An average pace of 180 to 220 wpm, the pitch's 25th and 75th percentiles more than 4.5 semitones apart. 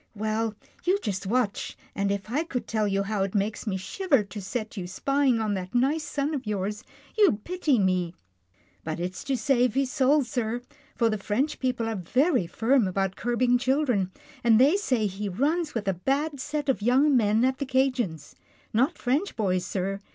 Yes: average, 190 wpm; average, 5.3 semitones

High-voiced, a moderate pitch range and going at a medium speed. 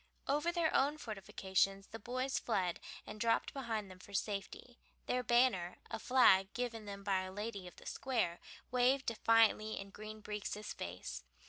Yes: high, 215 Hz; average, 4.1 semitones; average, 160 wpm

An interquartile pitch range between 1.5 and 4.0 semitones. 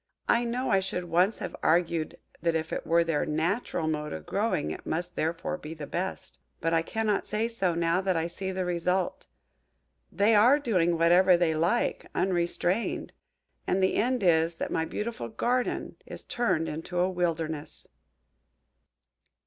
Yes: average, 2.9 semitones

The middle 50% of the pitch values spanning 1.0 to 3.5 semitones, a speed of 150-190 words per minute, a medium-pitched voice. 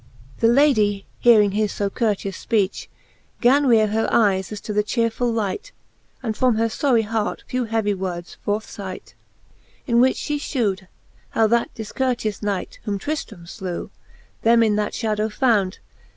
No: narrow, 2.6 semitones; average, 160 wpm; high, 220 Hz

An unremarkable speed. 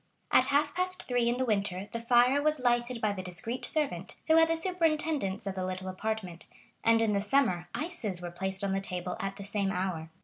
No: fast, 215 wpm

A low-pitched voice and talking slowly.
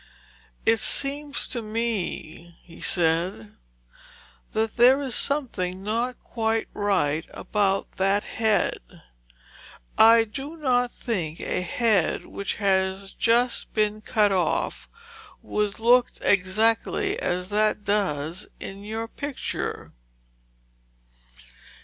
No: high, 210 Hz; slow, 100 wpm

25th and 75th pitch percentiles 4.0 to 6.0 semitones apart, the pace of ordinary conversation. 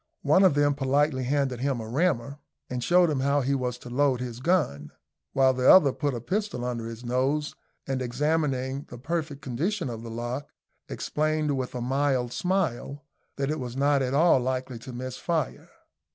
No: average, 3.0 semitones; average, 185 wpm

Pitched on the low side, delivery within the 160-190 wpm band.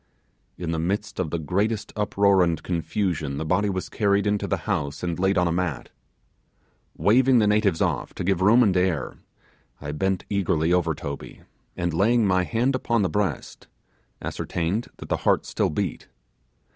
Yes: very low, 95 Hz; average, 170 wpm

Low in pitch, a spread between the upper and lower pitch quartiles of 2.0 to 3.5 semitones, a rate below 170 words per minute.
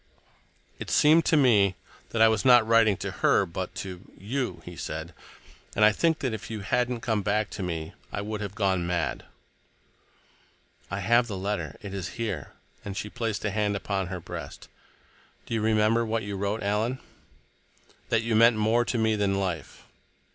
No: low, 105 Hz; narrow, 2.6 semitones; average, 185 wpm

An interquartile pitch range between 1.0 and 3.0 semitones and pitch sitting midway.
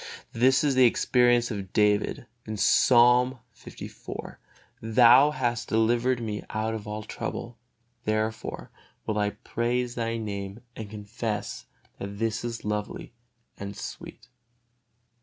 No: narrow, 2.4 semitones; low, 115 Hz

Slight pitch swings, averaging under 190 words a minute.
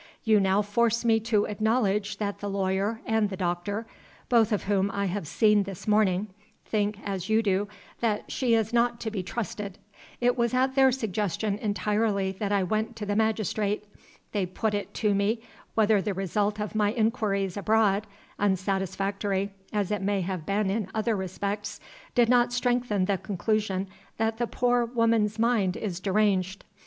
Yes: narrow, 2.2 semitones; average, 170 wpm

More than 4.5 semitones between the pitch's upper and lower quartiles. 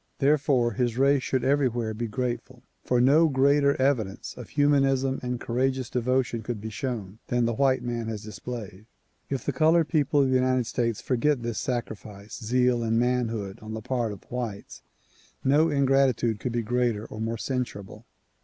No: average, 2.9 semitones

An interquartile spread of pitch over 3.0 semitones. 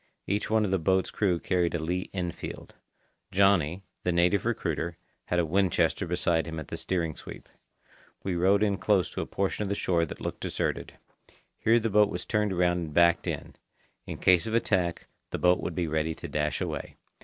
No: narrow, 2.6 semitones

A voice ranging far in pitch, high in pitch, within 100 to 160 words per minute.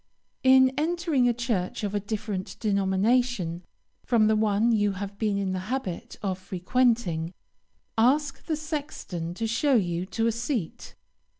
No: average, 4.9 semitones; high, 215 Hz; average, 145 wpm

